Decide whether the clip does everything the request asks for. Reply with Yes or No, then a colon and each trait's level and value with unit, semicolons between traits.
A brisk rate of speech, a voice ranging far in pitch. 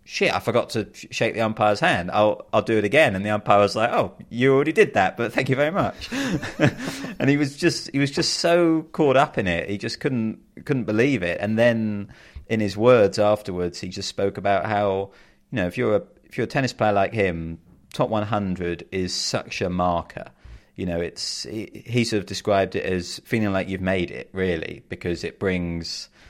No: fast, 215 wpm; average, 3.9 semitones